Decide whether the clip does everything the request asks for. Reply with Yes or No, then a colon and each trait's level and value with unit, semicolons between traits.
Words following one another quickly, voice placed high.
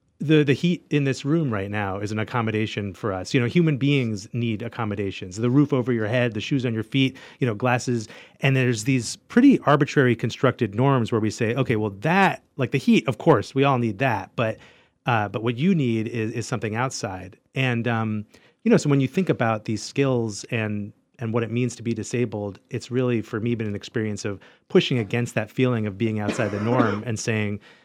No: fast, 220 wpm; low, 120 Hz